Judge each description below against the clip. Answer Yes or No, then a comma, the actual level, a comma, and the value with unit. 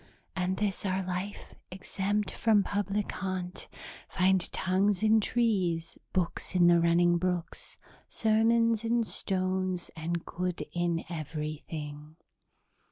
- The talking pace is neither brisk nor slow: No, slow, 110 wpm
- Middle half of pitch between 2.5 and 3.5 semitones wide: Yes, average, 2.9 semitones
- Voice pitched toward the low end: No, medium, 185 Hz